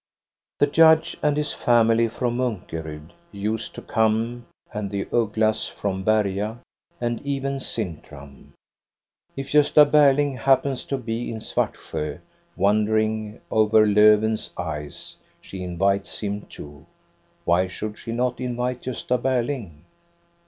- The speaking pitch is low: Yes, low, 110 Hz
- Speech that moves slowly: Yes, slow, 125 wpm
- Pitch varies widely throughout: No, average, 4.0 semitones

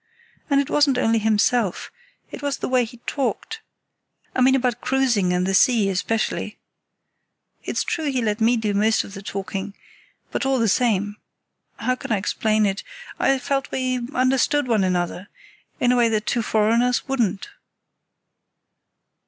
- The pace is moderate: Yes, average, 155 wpm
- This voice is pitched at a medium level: No, high, 230 Hz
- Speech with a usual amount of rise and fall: Yes, average, 3.8 semitones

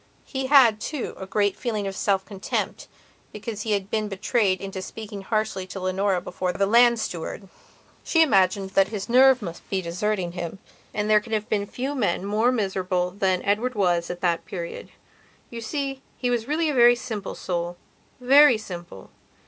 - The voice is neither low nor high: No, high, 205 Hz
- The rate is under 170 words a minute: No, average, 175 wpm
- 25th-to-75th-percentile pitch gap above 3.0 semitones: Yes, average, 4.0 semitones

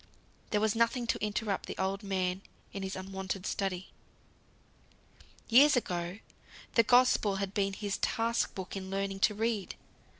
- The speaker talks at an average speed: Yes, average, 145 wpm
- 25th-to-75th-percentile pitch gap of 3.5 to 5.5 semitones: No, average, 2.7 semitones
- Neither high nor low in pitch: No, high, 195 Hz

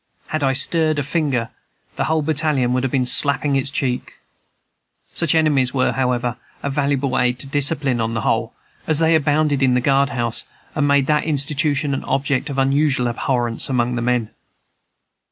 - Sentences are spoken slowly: No, average, 175 wpm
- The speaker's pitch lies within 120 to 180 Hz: Yes, low, 135 Hz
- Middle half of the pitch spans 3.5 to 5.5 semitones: No, average, 2.8 semitones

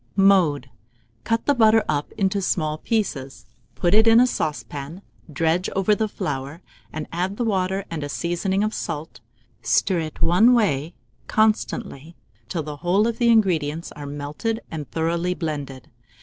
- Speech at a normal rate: Yes, average, 155 wpm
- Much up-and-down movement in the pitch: Yes, wide, 5.9 semitones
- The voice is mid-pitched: Yes, medium, 175 Hz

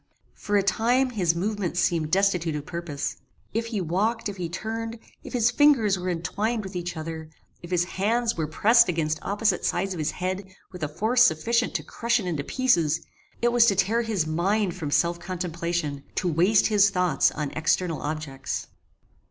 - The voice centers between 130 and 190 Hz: Yes, medium, 185 Hz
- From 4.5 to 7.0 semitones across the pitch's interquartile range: Yes, average, 4.9 semitones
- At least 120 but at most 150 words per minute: No, average, 185 wpm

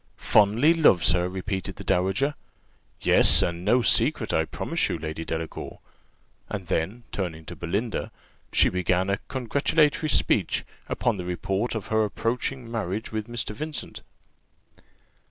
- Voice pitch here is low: Yes, low, 100 Hz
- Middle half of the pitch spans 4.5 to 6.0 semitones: Yes, average, 5.2 semitones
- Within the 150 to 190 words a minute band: No, slow, 135 wpm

